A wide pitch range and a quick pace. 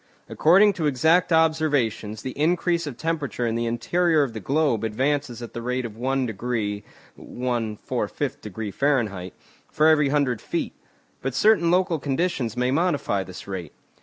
No: wide, 5.7 semitones; average, 155 wpm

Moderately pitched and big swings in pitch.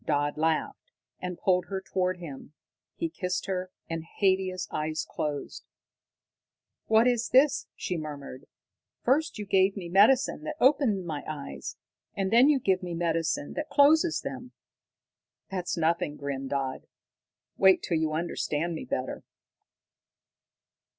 Yes: medium, 180 Hz; wide, 6.0 semitones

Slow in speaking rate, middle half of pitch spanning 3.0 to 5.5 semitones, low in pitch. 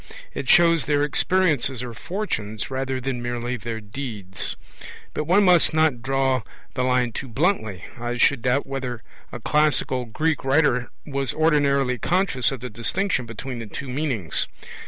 No: average, 155 wpm; average, 3.8 semitones; low, 130 Hz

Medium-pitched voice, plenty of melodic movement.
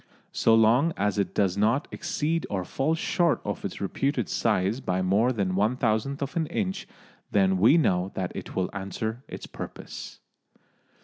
No: low, 110 Hz; wide, 6.3 semitones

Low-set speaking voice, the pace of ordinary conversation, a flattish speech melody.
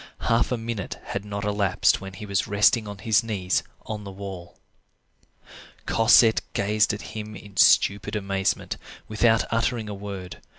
Yes: low, 105 Hz; average, 155 wpm; narrow, 2.0 semitones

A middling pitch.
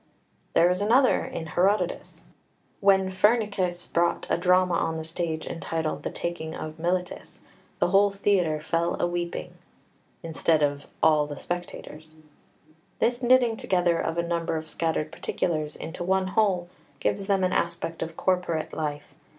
Yes: medium, 175 Hz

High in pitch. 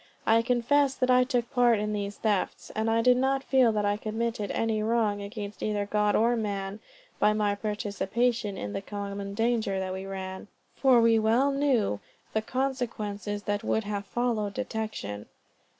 Yes: high, 215 Hz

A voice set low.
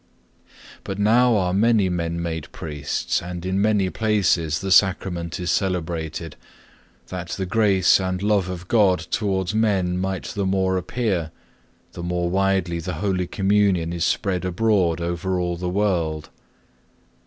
Yes: very low, 90 Hz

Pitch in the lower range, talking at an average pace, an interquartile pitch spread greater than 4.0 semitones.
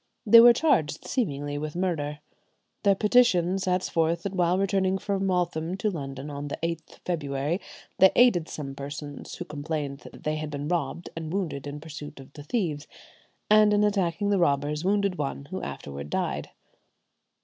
No: medium, 165 Hz; average, 170 wpm; average, 4.8 semitones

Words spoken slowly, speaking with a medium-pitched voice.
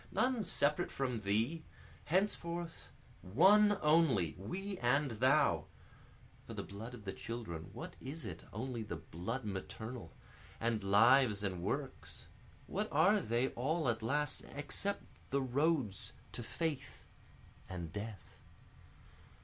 No: slow, 125 wpm; low, 125 Hz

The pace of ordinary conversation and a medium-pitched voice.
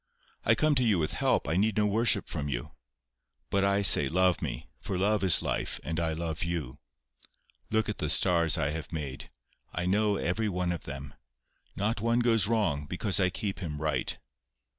No: average, 190 wpm; very low, 90 Hz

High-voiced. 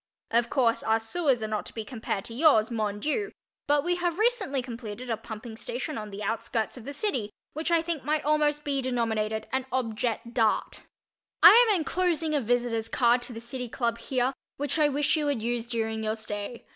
Yes: high, 245 Hz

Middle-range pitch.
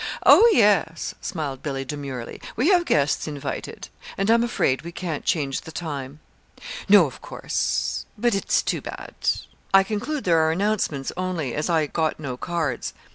Yes: medium, 160 Hz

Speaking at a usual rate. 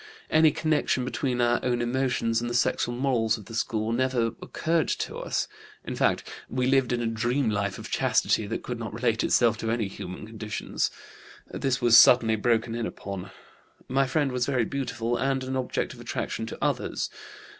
Yes: average, 180 wpm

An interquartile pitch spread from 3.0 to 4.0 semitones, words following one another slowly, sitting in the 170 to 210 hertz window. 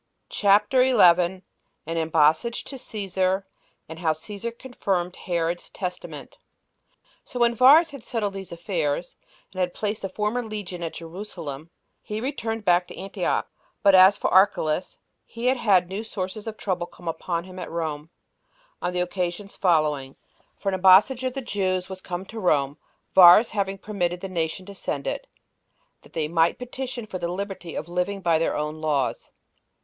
No: average, 3.7 semitones; average, 165 wpm; medium, 185 Hz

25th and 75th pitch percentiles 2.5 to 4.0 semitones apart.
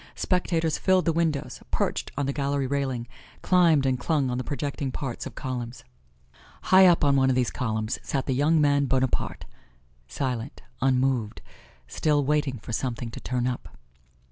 Yes: average, 3.0 semitones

